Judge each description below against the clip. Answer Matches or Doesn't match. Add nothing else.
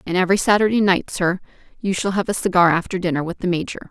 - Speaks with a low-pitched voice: Doesn't match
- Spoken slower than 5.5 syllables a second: Doesn't match